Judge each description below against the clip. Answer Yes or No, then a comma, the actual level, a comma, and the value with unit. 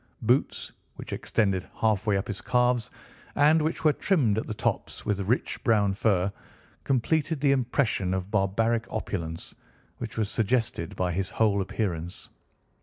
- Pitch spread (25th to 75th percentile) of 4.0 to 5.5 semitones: Yes, average, 4.3 semitones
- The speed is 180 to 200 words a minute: No, average, 145 wpm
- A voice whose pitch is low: Yes, low, 110 Hz